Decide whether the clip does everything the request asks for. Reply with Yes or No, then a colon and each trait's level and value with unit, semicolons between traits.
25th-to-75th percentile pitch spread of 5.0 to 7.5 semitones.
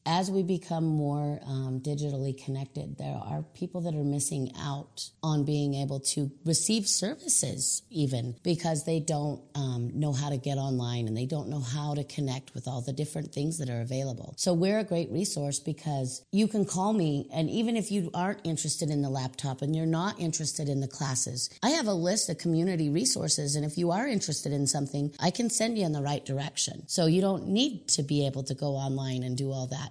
No: average, 3.7 semitones